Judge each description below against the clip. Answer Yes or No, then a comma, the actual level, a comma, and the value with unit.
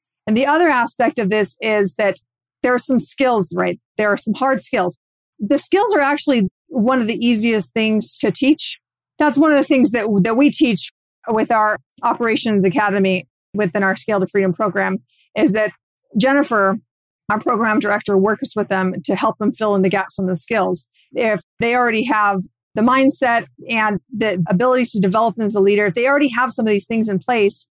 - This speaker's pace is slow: No, average, 200 wpm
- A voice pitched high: Yes, high, 215 Hz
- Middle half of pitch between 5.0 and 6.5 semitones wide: No, average, 4.0 semitones